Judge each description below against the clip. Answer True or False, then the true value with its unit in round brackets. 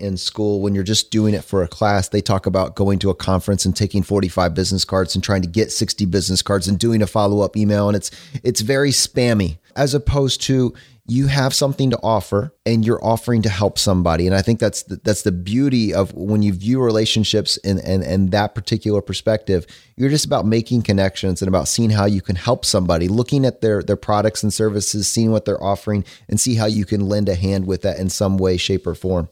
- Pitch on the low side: True (105 Hz)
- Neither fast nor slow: False (225 wpm)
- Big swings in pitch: False (2.8 semitones)